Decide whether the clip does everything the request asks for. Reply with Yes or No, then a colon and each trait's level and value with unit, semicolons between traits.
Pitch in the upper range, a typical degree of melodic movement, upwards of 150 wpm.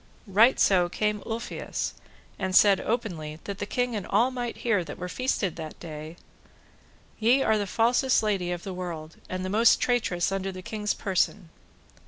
Yes: high, 195 Hz; average, 4.1 semitones; average, 175 wpm